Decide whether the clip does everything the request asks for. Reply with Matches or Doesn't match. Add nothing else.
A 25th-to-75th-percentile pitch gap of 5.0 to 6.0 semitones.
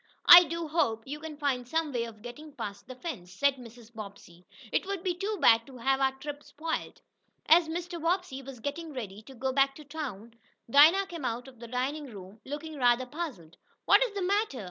Matches